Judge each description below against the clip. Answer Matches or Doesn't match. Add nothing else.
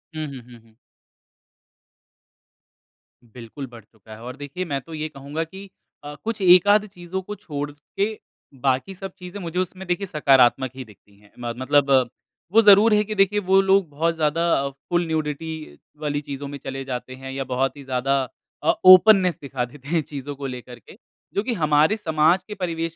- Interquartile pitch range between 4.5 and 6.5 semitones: Matches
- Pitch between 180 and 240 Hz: Doesn't match